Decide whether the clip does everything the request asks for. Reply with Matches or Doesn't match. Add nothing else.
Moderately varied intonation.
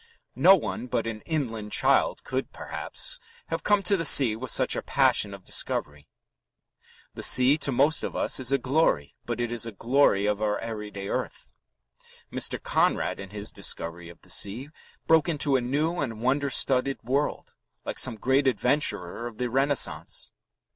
Matches